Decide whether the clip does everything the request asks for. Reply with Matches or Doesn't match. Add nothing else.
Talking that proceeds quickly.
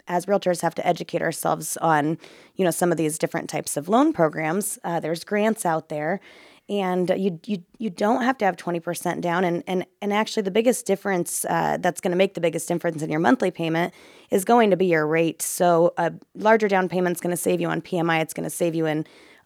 Matches